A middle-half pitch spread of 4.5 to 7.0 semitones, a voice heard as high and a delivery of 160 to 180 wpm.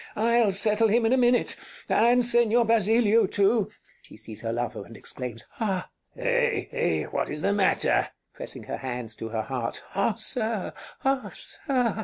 Yes: average, 5.1 semitones; high, 220 Hz; average, 175 wpm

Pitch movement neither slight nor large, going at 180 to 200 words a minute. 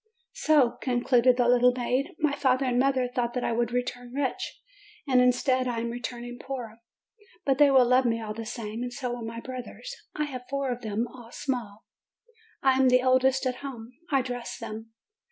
No: narrow, 1.6 semitones; average, 190 wpm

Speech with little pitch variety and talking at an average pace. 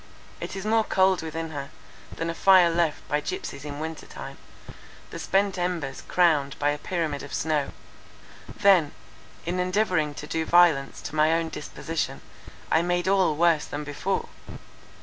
No: average, 3.4 semitones; average, 160 wpm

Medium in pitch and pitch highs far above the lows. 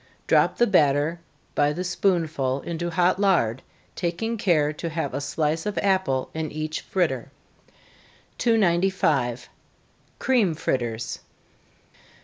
No: medium, 165 Hz; average, 4.6 semitones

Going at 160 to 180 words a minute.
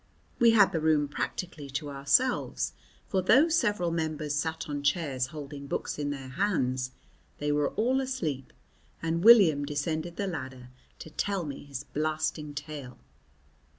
No: average, 150 wpm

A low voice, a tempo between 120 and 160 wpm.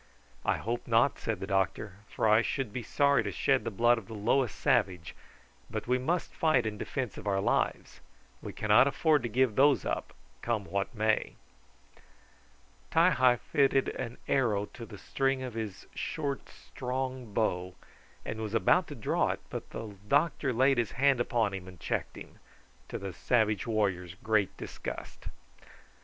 No: low, 115 Hz; average, 170 wpm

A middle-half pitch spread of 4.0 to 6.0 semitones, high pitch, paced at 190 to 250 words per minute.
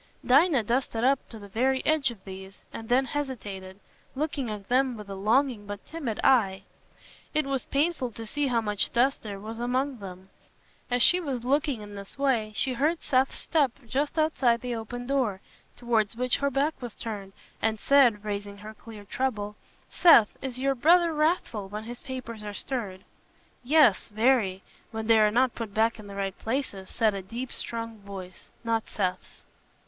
No: average, 4.4 semitones; high, 235 Hz; average, 180 wpm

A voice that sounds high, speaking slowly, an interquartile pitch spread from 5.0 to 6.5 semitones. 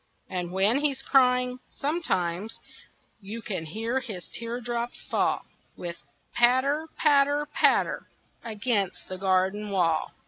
Yes: high, 230 Hz; slow, 115 wpm; wide, 5.6 semitones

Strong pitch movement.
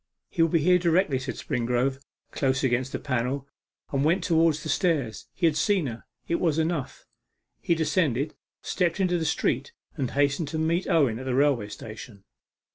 No: average, 4.3 semitones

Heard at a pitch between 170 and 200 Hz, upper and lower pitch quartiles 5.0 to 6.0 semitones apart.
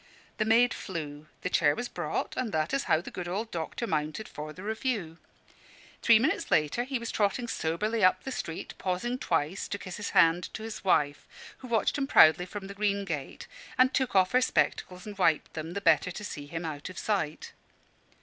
Yes: high, 190 Hz; wide, 5.6 semitones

